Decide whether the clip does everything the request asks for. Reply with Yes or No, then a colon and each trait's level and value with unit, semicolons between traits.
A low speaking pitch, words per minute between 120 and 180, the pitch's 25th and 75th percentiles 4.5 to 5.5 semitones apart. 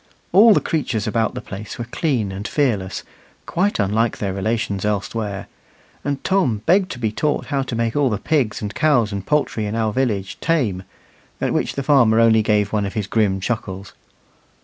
No: low, 110 Hz; average, 190 wpm; average, 4.9 semitones